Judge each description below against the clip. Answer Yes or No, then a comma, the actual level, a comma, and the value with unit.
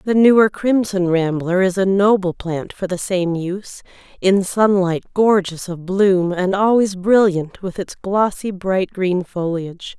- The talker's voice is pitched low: No, high, 190 Hz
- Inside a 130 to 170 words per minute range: Yes, average, 155 wpm